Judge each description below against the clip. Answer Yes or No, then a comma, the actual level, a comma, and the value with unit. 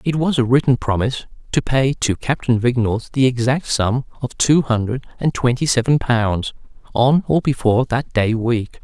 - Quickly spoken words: No, average, 175 wpm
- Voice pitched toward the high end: No, low, 125 Hz